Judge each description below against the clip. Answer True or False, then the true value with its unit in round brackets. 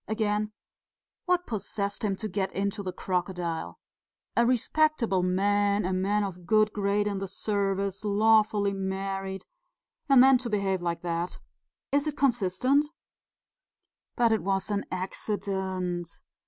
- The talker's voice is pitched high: True (200 Hz)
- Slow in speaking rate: True (130 wpm)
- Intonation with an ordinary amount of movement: False (2.3 semitones)